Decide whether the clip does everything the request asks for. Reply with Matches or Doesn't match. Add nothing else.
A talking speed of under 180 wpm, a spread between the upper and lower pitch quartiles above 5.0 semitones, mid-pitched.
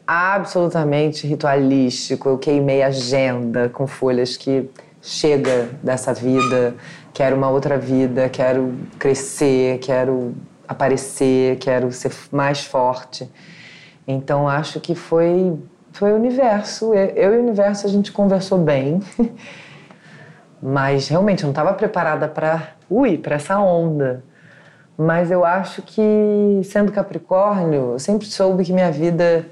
Matches